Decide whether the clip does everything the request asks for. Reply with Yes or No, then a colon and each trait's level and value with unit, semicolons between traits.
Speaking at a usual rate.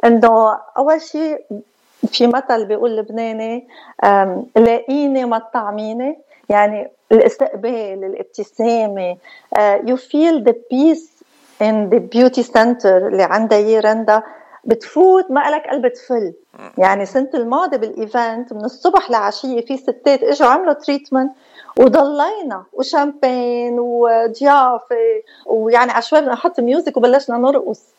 Yes: average, 110 wpm